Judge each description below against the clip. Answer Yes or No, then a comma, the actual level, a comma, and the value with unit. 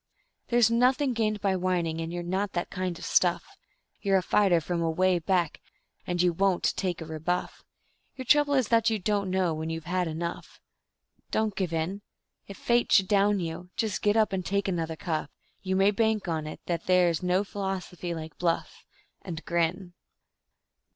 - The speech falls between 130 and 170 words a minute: No, average, 185 wpm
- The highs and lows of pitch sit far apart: No, average, 3.1 semitones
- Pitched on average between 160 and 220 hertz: Yes, medium, 185 Hz